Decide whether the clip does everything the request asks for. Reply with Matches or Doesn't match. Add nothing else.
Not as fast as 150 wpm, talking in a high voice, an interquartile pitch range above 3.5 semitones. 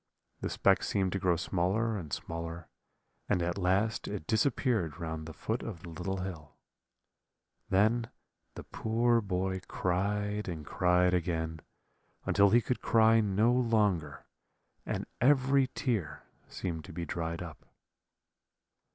Doesn't match